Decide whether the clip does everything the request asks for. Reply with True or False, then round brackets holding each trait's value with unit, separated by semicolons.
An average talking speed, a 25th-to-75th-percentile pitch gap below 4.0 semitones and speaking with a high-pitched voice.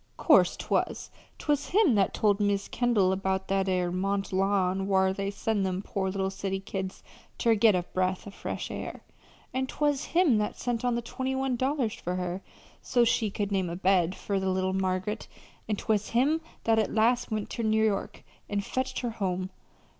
True (190 wpm; 3.6 semitones; 200 Hz)